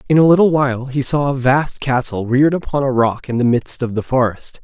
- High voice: No, low, 130 Hz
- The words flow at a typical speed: No, fast, 245 wpm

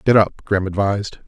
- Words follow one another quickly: No, average, 190 wpm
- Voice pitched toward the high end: No, low, 100 Hz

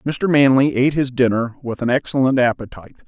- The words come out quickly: No, average, 175 wpm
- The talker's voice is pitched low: Yes, low, 130 Hz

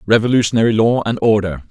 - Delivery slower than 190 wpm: Yes, average, 140 wpm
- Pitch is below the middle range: Yes, low, 110 Hz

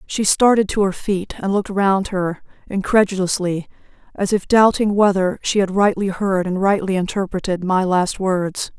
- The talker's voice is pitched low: No, high, 190 Hz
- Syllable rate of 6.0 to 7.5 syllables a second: No, 4.7 syllables/s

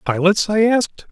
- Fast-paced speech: No, average, 160 wpm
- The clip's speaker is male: Yes, male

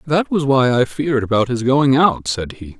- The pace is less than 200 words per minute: No, fast, 235 wpm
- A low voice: Yes, low, 130 Hz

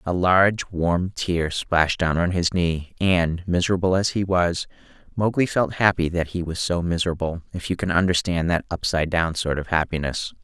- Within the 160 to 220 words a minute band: Yes, average, 180 wpm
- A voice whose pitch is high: No, very low, 85 Hz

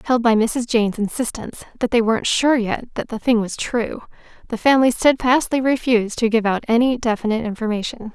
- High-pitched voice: Yes, high, 230 Hz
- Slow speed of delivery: No, average, 185 wpm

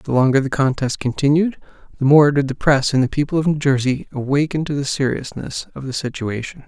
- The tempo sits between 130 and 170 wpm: No, fast, 205 wpm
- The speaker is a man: Yes, male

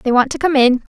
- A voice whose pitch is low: No, very high, 265 Hz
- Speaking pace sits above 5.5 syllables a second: Yes, 6.1 syllables/s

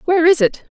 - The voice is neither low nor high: No, very high, 315 Hz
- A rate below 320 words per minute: Yes, fast, 240 wpm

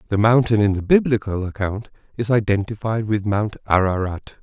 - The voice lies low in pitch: Yes, low, 105 Hz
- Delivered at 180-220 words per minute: No, average, 150 wpm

